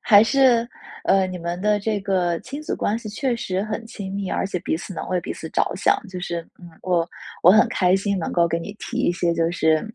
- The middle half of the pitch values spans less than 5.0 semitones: Yes, average, 3.5 semitones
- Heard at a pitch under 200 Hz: Yes, high, 190 Hz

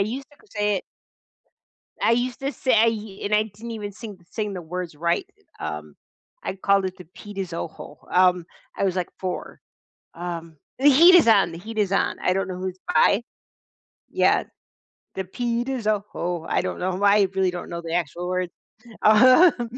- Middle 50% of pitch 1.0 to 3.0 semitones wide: No, average, 3.9 semitones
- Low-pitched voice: No, high, 195 Hz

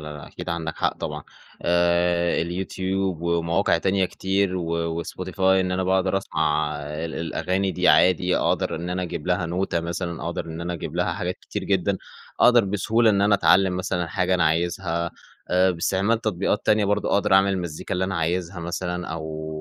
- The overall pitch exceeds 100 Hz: No, very low, 90 Hz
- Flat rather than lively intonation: Yes, narrow, 2.2 semitones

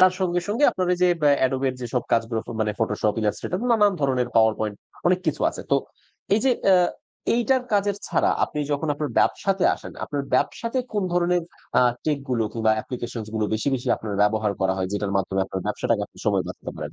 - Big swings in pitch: Yes, wide, 8.9 semitones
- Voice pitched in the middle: No, low, 130 Hz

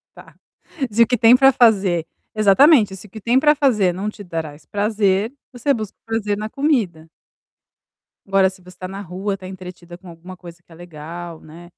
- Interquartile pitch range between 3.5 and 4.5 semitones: Yes, average, 4.1 semitones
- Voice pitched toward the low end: No, high, 195 Hz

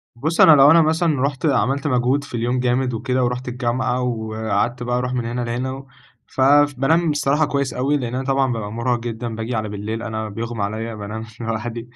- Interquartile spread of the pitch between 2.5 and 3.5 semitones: Yes, average, 2.9 semitones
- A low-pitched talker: Yes, low, 125 Hz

